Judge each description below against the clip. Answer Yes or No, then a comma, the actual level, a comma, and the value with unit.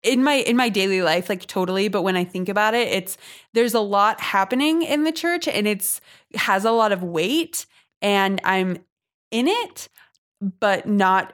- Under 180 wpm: No, average, 190 wpm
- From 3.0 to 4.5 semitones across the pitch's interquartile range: No, average, 4.9 semitones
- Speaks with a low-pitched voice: No, high, 205 Hz